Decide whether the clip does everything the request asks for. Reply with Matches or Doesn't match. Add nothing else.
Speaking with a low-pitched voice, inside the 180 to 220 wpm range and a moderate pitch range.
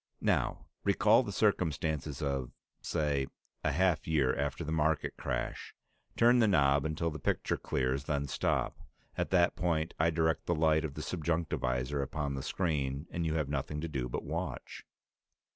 Doesn't match